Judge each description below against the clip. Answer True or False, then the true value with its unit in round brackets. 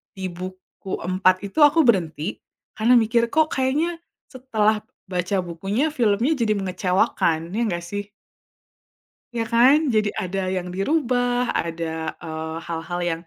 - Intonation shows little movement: False (5.4 semitones)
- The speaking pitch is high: True (195 Hz)